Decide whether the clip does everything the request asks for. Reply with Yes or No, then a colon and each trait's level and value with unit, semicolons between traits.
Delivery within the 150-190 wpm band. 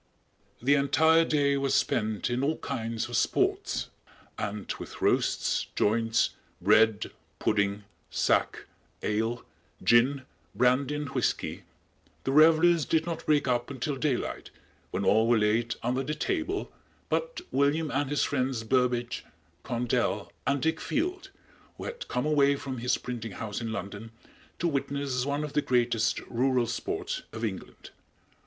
No: average, 140 wpm